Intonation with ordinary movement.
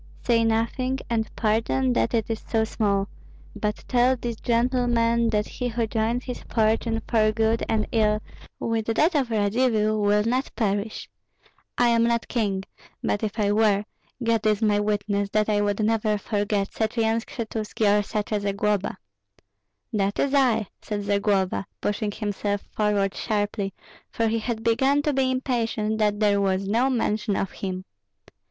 No: narrow, 2.1 semitones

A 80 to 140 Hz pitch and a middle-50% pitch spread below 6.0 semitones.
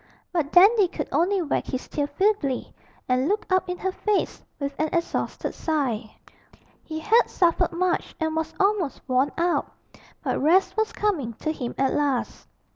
No: very high, 325 Hz; average, 5.2 semitones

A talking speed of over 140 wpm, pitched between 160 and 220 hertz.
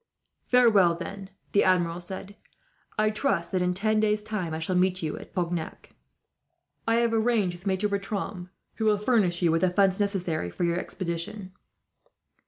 Yes: average, 170 wpm; high, 190 Hz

